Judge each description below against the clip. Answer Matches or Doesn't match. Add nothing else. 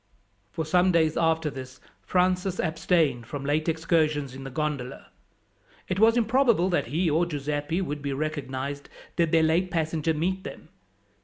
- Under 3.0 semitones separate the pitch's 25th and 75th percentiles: Doesn't match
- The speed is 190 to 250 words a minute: Doesn't match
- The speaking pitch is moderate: Matches